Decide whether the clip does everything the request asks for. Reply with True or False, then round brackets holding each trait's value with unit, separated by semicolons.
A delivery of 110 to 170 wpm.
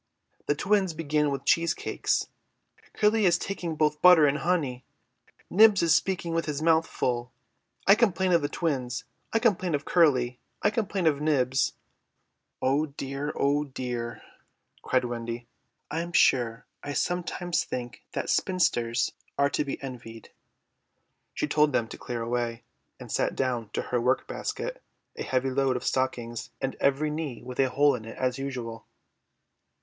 True (155 wpm)